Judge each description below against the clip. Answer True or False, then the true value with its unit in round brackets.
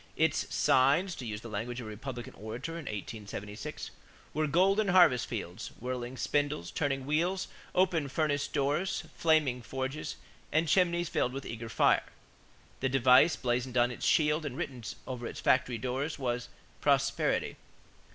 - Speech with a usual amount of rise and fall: True (4.4 semitones)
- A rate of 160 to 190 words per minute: False (150 wpm)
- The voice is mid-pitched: False (130 Hz)